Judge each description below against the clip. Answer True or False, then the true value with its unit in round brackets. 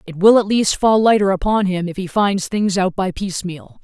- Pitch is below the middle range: False (195 Hz)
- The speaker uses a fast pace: True (235 wpm)